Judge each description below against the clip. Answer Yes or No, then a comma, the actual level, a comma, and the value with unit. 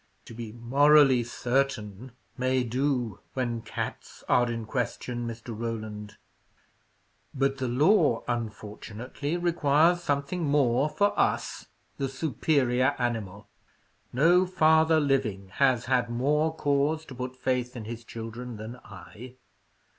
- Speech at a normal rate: No, slow, 120 wpm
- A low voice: Yes, low, 125 Hz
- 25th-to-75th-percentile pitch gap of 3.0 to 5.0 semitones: Yes, average, 3.7 semitones